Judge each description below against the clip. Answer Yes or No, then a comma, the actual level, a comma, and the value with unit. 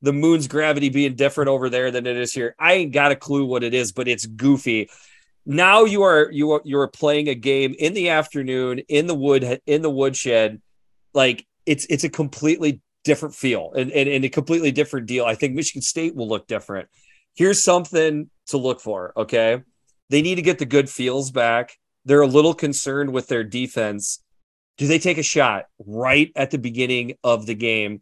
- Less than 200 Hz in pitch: Yes, medium, 140 Hz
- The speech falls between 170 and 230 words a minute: Yes, fast, 205 wpm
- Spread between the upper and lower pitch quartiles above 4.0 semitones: No, average, 3.4 semitones